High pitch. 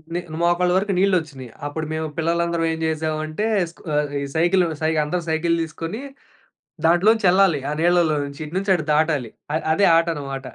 No: medium, 165 Hz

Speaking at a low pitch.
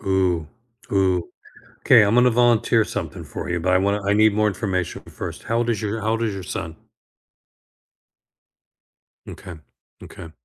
Yes: low, 100 Hz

